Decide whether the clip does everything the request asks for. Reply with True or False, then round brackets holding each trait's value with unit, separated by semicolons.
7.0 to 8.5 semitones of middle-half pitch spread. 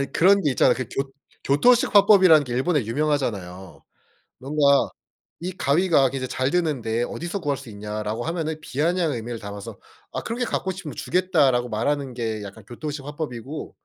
False (5.4 semitones)